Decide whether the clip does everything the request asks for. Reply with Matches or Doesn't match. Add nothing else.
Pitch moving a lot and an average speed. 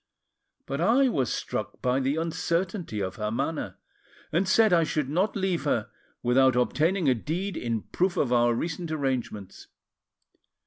Matches